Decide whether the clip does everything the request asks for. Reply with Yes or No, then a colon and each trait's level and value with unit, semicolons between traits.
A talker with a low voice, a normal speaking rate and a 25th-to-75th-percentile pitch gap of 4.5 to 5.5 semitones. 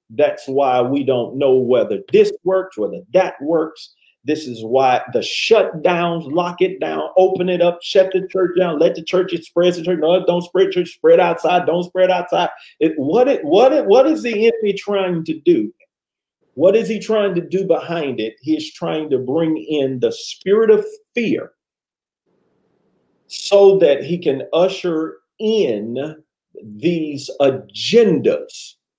No: medium, 180 Hz; average, 160 wpm; average, 5.2 semitones